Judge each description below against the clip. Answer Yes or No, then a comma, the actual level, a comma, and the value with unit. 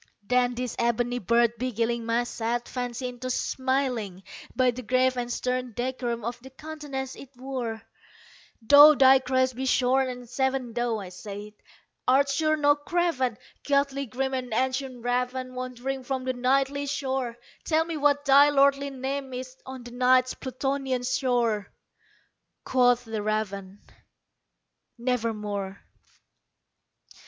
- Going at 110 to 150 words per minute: Yes, slow, 135 wpm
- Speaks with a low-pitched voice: No, very high, 255 Hz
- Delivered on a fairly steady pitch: Yes, narrow, 2.0 semitones